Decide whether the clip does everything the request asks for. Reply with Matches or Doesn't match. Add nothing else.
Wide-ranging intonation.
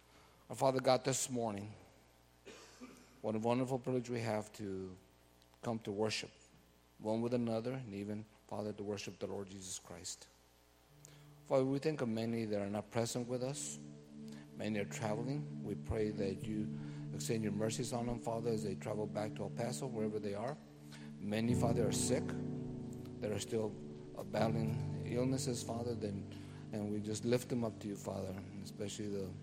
Matches